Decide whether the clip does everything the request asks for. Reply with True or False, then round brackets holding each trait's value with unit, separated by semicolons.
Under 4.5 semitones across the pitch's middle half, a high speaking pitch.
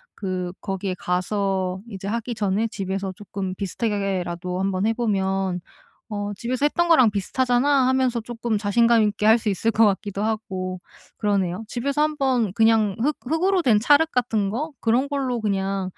True (4.0 semitones; 215 Hz)